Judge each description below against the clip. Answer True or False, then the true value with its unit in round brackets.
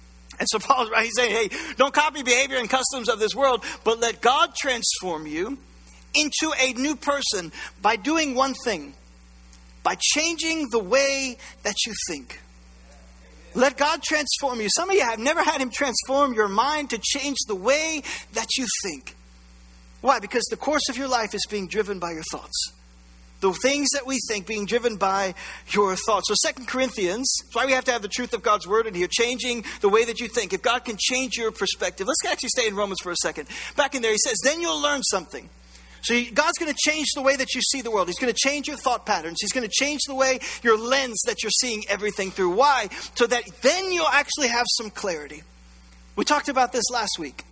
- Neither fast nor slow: False (210 wpm)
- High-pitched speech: True (240 Hz)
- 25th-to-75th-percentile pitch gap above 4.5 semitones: True (5.2 semitones)